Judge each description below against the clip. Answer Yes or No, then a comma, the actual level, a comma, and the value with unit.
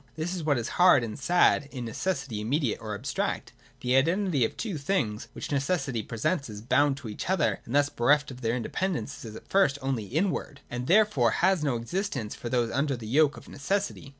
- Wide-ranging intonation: Yes, wide, 5.8 semitones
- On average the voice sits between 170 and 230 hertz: No, medium, 140 Hz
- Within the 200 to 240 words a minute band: Yes, fast, 205 wpm